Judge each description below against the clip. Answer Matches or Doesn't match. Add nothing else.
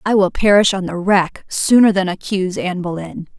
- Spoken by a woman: Matches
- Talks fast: Doesn't match